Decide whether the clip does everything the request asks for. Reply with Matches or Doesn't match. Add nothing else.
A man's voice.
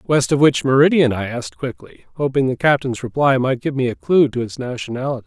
Matches